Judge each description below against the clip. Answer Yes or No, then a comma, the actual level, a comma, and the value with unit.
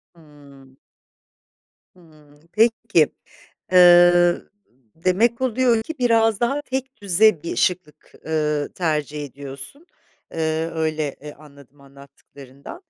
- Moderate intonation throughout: No, wide, 7.0 semitones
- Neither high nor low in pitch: Yes, medium, 160 Hz